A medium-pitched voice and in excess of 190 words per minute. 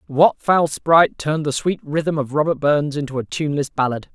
Yes: medium, 150 Hz; fast, 205 wpm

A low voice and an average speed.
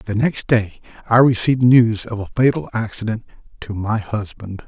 Yes: low, 110 Hz; average, 165 wpm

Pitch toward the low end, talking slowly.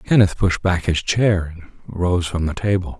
No: very low, 90 Hz; average, 200 wpm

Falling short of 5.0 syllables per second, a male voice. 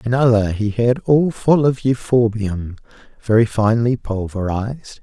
Yes: 4.4 syllables/s; male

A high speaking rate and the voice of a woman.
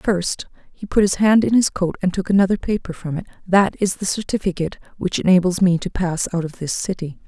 Yes: fast, 225 wpm; female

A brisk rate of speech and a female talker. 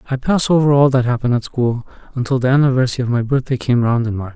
No: fast, 250 wpm; male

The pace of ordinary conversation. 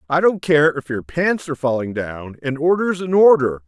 No: fast, 215 wpm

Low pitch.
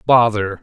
Yes: low, 110 Hz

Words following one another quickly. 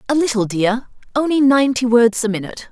No: average, 175 wpm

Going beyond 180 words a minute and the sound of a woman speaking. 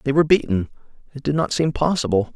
No: fast, 205 wpm; male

